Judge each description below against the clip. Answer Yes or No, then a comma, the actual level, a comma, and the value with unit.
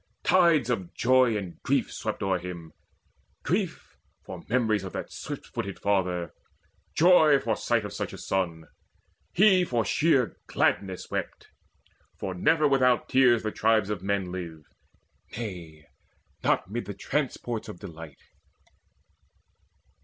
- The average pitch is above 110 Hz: No, low, 105 Hz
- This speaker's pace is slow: Yes, slow, 130 wpm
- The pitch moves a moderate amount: No, wide, 5.7 semitones